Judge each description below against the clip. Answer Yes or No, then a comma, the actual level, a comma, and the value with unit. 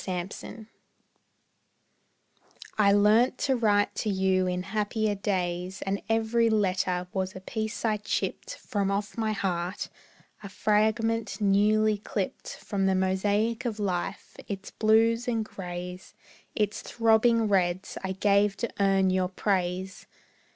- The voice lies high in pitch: Yes, high, 205 Hz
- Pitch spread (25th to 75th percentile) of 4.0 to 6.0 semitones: No, narrow, 2.5 semitones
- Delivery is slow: Yes, slow, 130 wpm